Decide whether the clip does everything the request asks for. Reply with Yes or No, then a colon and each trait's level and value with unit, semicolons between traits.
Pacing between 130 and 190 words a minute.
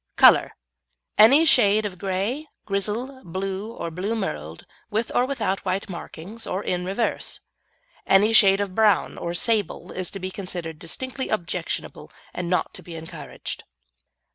Yes: average, 140 wpm